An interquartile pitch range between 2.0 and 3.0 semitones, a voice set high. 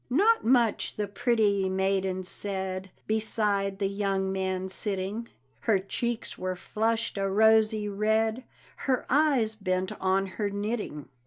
Yes: narrow, 2.6 semitones; high, 205 Hz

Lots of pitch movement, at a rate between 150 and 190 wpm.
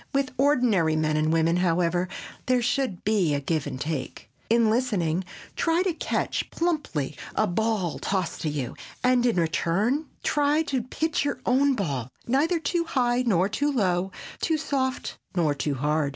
Yes: wide, 8.7 semitones; average, 160 wpm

